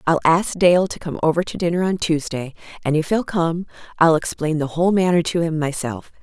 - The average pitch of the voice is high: No, medium, 165 Hz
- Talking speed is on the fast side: Yes, fast, 210 wpm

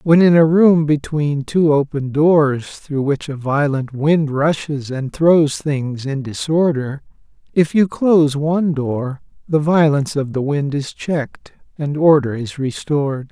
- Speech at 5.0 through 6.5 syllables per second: No, 4.0 syllables/s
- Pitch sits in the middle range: Yes, medium, 145 Hz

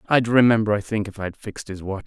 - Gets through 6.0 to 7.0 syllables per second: Yes, 6.7 syllables/s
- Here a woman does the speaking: No, male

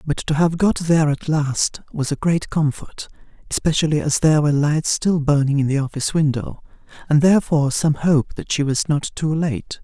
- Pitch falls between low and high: Yes, medium, 150 Hz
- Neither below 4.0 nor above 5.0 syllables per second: No, 5.3 syllables/s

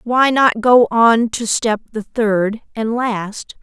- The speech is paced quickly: No, average, 165 wpm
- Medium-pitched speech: No, high, 225 Hz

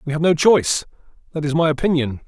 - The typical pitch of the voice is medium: Yes, medium, 155 Hz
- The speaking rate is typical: No, fast, 210 wpm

